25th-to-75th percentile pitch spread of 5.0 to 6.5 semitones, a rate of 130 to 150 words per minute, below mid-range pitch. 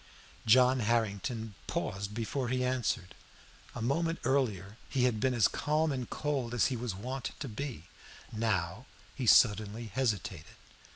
No: average, 3.7 semitones; average, 140 wpm; low, 120 Hz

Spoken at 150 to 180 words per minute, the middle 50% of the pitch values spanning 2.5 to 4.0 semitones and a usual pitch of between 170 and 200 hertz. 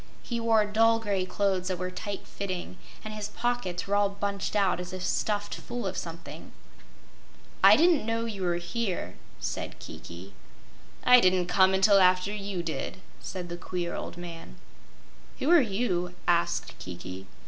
Yes: average, 160 wpm; average, 3.2 semitones; high, 190 Hz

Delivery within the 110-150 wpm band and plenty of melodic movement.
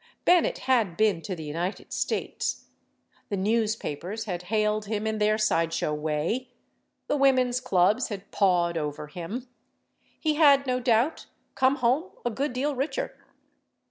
Yes: average, 145 wpm; wide, 6.3 semitones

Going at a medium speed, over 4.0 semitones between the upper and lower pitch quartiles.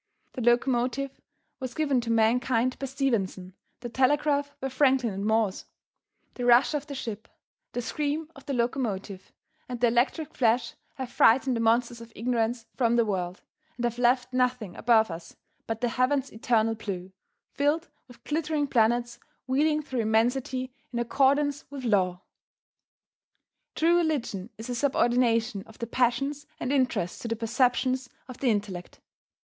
No: average, 155 wpm; average, 3.0 semitones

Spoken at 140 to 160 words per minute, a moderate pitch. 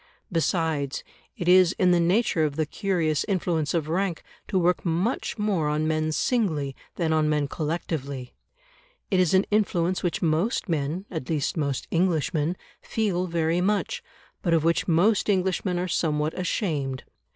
Yes: average, 155 wpm; medium, 170 Hz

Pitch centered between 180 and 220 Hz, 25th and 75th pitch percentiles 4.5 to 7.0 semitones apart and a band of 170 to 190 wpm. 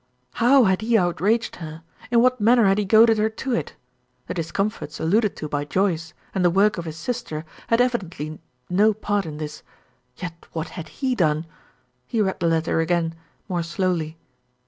Yes: medium, 185 Hz; average, 5.1 semitones; average, 180 wpm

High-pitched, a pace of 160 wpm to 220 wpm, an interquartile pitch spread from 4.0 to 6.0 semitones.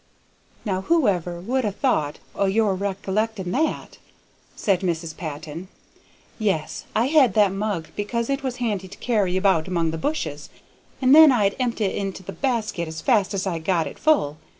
Yes: high, 195 Hz; average, 175 wpm; average, 4.8 semitones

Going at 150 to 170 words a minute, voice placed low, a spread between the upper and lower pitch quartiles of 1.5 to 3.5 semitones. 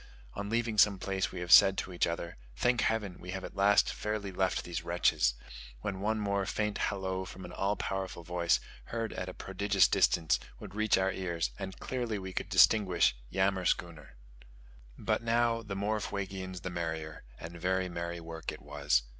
No: average, 180 wpm; very low, 95 Hz; average, 2.8 semitones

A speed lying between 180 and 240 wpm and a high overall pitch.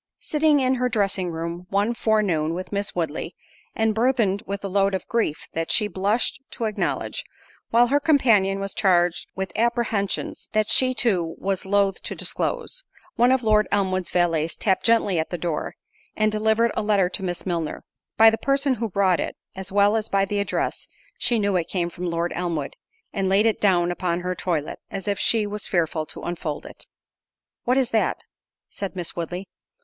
Yes: average, 185 wpm; high, 200 Hz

